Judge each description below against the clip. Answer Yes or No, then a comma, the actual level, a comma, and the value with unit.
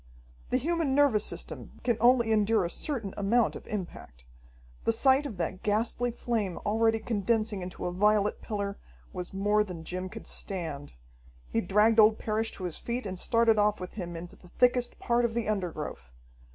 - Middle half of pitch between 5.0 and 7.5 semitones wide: No, average, 3.9 semitones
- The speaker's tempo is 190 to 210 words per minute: No, average, 180 wpm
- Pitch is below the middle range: No, high, 210 Hz